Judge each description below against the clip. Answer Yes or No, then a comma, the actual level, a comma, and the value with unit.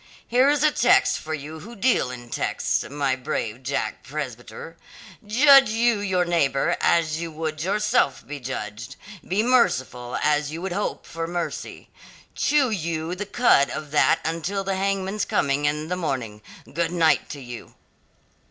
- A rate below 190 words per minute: Yes, average, 160 wpm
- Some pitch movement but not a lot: No, wide, 6.4 semitones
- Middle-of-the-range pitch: Yes, medium, 165 Hz